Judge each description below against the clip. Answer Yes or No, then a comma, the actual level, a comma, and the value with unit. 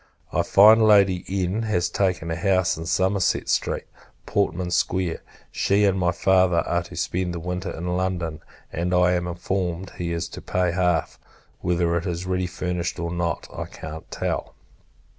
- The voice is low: Yes, very low, 90 Hz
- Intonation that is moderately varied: No, narrow, 1.5 semitones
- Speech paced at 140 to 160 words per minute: No, average, 170 wpm